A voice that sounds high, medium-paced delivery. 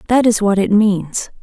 No: high, 205 Hz; fast, 210 wpm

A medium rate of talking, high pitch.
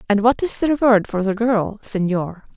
No: fast, 210 wpm; high, 215 Hz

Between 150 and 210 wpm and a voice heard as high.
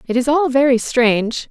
Yes: average, 200 wpm; very high, 255 Hz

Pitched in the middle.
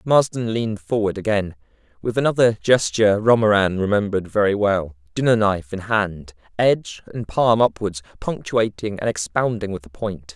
No: low, 105 Hz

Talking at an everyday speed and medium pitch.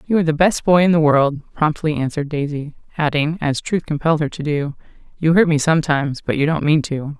No: fast, 225 wpm; medium, 155 Hz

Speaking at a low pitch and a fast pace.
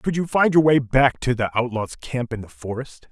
Yes: low, 130 Hz; fast, 250 wpm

